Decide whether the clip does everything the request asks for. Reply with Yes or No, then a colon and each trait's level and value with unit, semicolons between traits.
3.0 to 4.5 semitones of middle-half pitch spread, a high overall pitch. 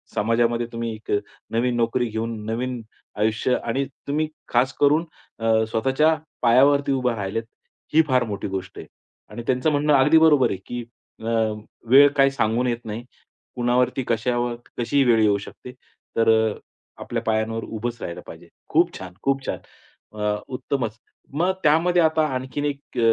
No: average, 3.5 semitones; low, 120 Hz